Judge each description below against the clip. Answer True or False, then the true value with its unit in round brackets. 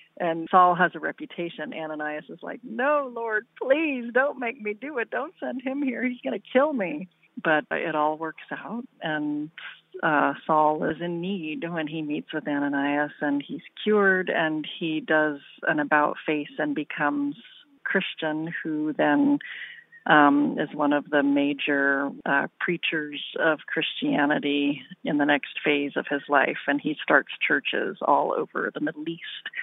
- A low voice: False (160 Hz)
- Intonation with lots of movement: True (8.3 semitones)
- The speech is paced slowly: False (165 wpm)